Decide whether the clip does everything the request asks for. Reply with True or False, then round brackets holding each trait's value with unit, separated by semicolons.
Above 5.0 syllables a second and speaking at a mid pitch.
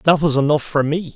True (5.8 syllables/s; 150 Hz)